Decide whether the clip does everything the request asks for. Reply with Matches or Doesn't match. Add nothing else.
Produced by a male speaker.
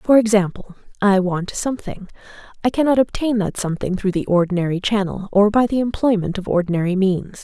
Doesn't match